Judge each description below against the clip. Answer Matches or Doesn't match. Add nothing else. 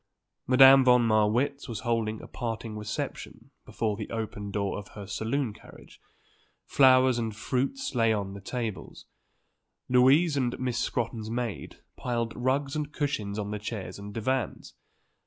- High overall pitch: Doesn't match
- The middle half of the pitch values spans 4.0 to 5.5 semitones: Doesn't match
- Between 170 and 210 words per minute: Doesn't match